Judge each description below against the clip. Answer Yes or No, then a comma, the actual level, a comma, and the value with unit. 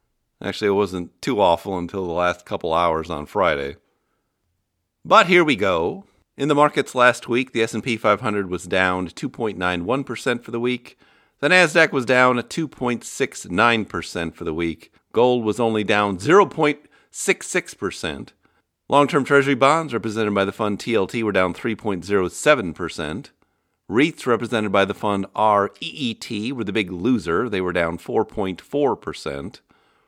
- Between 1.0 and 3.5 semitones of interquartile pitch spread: No, average, 5.1 semitones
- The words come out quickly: No, average, 150 wpm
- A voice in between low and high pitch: No, low, 105 Hz